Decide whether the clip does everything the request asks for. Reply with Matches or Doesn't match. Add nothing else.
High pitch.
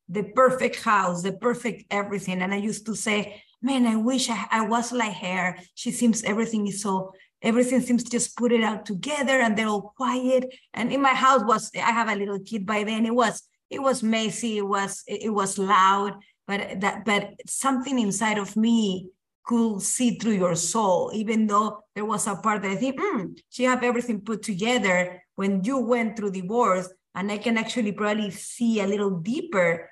Matches